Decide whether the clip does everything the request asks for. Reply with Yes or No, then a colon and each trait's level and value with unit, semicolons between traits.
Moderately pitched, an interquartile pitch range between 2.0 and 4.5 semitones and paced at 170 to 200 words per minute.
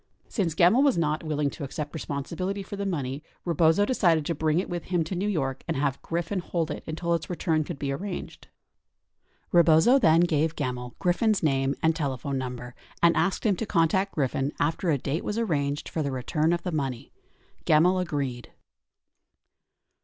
Yes: medium, 160 Hz; average, 3.9 semitones; average, 180 wpm